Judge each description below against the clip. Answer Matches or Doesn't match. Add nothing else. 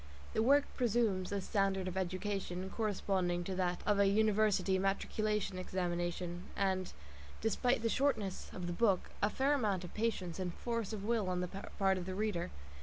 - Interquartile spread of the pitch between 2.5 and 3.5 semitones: Matches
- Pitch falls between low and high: Doesn't match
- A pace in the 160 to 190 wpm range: Matches